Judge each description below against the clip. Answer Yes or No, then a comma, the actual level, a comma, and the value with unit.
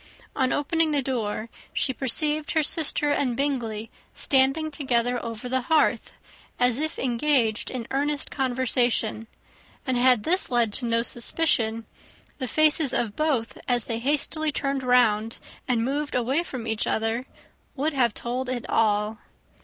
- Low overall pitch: No, very high, 255 Hz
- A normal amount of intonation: Yes, average, 3.9 semitones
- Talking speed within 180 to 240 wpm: No, average, 145 wpm